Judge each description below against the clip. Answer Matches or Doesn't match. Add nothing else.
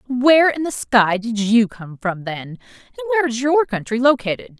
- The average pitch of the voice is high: Matches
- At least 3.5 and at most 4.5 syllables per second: Doesn't match